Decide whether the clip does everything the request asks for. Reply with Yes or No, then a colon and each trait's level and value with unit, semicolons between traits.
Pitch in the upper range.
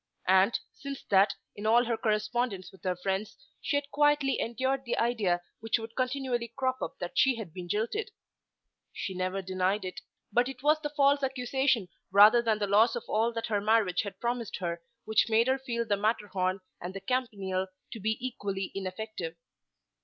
Yes: high, 220 Hz